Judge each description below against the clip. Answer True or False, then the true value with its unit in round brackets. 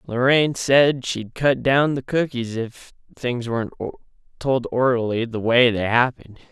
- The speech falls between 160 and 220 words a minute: False (145 wpm)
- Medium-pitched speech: False (125 Hz)